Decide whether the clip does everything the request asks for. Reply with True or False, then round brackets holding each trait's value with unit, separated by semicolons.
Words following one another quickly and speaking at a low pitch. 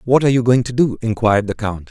True (285 wpm; 115 Hz)